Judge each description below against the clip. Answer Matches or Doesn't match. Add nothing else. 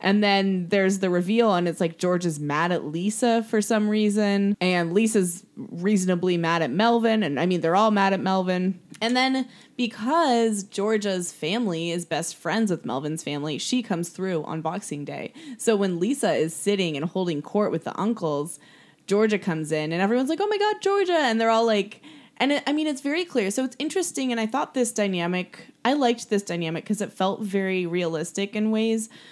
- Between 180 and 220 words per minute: Matches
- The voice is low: Doesn't match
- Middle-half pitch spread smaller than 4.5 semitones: Doesn't match